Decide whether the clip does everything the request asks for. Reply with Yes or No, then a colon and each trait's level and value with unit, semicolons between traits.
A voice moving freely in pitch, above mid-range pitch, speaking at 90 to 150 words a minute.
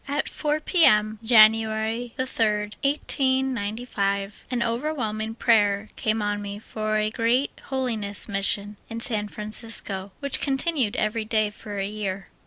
No: average, 2.9 semitones; high, 220 Hz; slow, 135 wpm